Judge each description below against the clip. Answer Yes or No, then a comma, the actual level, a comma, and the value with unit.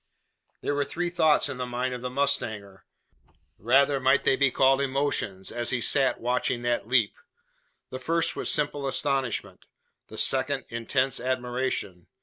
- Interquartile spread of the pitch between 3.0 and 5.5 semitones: No, narrow, 2.4 semitones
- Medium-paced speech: Yes, average, 150 wpm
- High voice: No, low, 130 Hz